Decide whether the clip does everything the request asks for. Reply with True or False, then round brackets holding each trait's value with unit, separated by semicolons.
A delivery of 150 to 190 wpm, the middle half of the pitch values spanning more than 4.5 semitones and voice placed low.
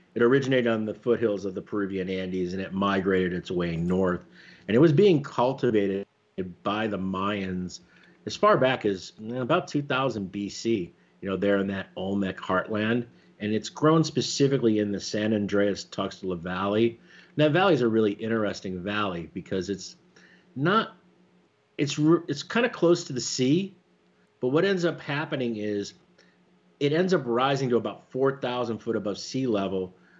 True (165 wpm; 5.5 semitones; 105 Hz)